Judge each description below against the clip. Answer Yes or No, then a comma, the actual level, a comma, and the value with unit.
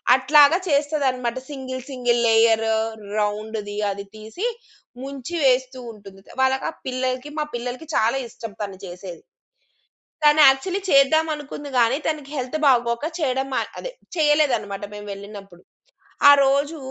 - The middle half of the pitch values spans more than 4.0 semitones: Yes, average, 4.4 semitones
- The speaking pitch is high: Yes, very high, 255 Hz